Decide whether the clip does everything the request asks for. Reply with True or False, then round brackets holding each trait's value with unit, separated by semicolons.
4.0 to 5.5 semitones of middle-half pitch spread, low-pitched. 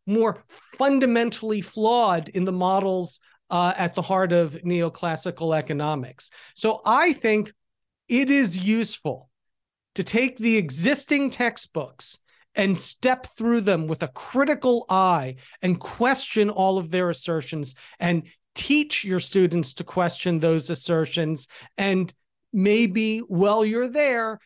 False (5.0 semitones; 190 Hz)